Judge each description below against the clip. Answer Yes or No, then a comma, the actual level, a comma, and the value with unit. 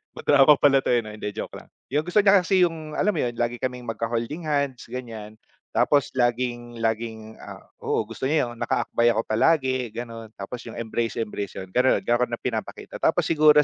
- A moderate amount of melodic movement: Yes, average, 4.1 semitones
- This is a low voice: Yes, low, 120 Hz